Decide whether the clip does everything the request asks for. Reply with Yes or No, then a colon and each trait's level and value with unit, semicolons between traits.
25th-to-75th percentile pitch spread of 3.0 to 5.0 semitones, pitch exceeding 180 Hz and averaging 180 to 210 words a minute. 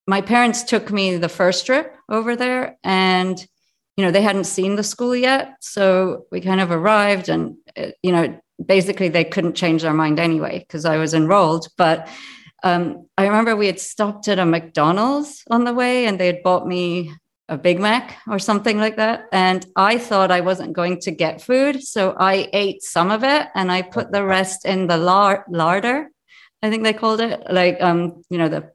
Yes: average, 3.6 semitones; high, 190 Hz; average, 200 wpm